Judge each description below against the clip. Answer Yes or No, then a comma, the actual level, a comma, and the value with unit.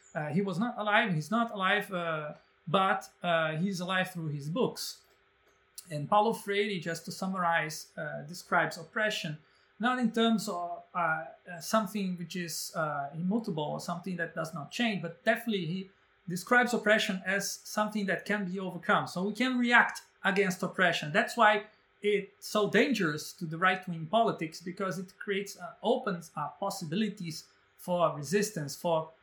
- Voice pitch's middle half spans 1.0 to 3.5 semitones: No, average, 3.9 semitones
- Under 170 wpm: Yes, average, 160 wpm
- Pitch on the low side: No, high, 190 Hz